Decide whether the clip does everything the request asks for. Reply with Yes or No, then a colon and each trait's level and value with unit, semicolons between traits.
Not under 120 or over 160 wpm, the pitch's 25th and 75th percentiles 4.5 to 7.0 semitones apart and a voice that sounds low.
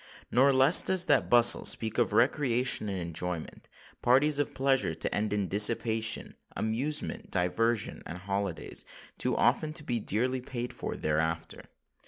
Yes: slow, 135 wpm; average, 5.2 semitones; low, 115 Hz